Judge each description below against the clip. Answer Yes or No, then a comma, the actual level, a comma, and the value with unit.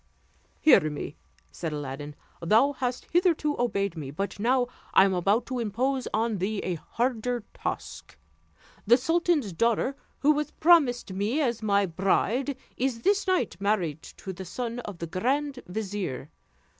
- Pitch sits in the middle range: No, high, 225 Hz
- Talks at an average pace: Yes, average, 150 wpm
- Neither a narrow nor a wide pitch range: No, wide, 5.8 semitones